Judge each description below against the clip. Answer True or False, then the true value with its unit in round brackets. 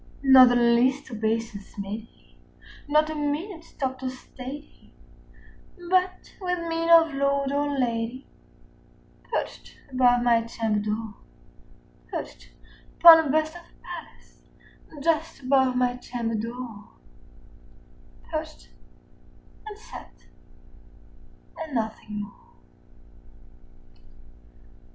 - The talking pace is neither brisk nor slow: False (105 wpm)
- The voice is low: False (260 Hz)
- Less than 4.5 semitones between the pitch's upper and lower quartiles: False (5.2 semitones)